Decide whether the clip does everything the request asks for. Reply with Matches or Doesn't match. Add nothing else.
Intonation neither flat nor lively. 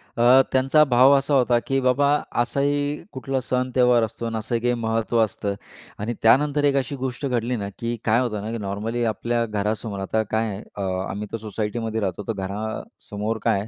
Matches